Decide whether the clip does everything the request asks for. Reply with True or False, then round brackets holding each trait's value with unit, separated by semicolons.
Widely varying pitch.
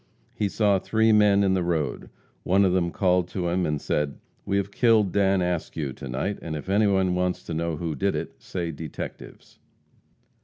False (3.2 semitones)